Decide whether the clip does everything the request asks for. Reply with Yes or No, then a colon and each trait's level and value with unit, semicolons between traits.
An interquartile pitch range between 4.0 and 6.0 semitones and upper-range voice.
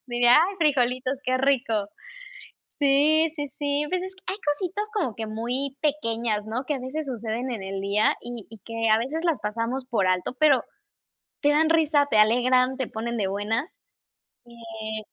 Yes: average, 4.6 semitones; very high, 255 Hz